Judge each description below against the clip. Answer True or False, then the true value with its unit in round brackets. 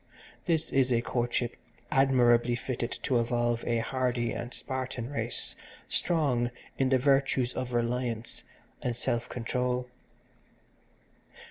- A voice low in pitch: True (125 Hz)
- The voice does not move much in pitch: True (1.6 semitones)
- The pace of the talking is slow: True (115 wpm)